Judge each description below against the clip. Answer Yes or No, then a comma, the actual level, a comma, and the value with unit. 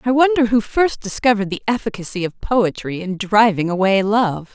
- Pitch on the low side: No, high, 215 Hz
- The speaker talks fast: No, average, 170 wpm